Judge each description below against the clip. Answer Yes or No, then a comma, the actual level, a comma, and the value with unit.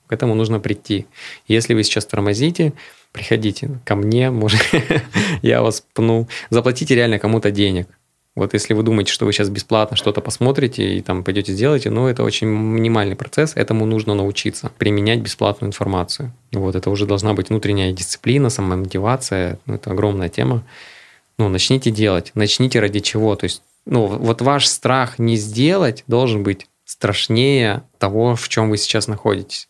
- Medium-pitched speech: No, low, 110 Hz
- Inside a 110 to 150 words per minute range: No, fast, 160 wpm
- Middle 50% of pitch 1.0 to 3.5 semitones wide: Yes, average, 3.1 semitones